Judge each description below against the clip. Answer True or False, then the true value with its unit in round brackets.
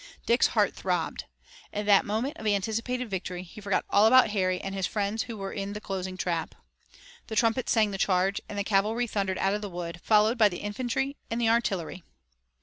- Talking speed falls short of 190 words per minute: False (205 wpm)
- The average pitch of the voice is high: True (205 Hz)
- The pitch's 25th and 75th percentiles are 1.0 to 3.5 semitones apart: True (2.7 semitones)